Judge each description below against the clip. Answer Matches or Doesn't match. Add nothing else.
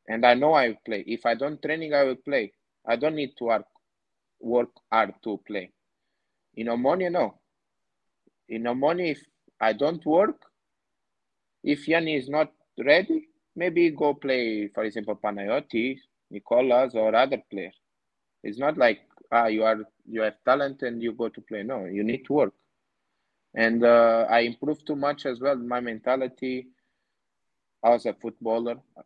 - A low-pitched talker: Matches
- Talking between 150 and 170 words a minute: Matches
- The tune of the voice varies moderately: Matches